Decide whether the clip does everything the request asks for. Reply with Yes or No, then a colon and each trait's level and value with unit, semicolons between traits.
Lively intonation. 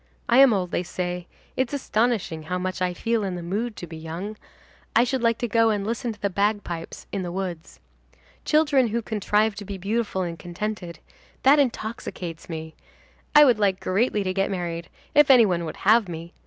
No: average, 4.7 semitones